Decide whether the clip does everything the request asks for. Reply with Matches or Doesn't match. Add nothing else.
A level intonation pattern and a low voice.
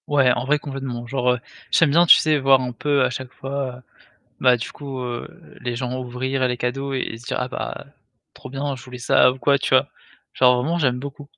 Matches